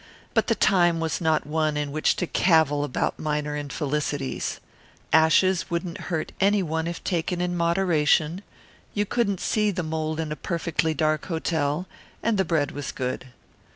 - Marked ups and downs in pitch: No, average, 2.9 semitones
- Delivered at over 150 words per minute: Yes, average, 160 wpm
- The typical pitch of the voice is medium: Yes, medium, 160 Hz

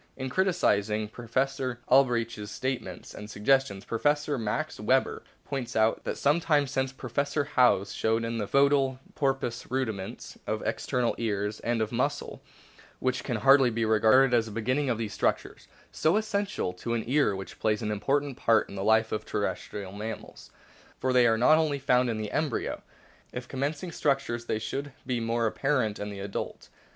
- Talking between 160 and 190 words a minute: Yes, average, 180 wpm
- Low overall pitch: Yes, low, 120 Hz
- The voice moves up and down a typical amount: Yes, average, 3.9 semitones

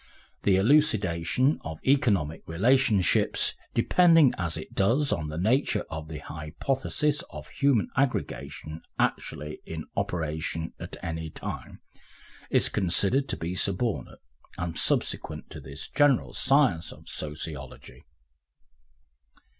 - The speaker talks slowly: Yes, slow, 115 wpm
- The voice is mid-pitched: No, very low, 95 Hz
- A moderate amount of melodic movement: No, wide, 8.9 semitones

